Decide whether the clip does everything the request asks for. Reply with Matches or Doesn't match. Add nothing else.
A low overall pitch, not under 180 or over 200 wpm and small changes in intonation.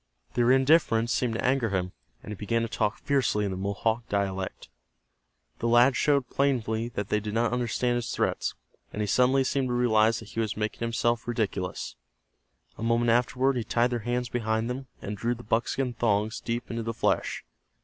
Matches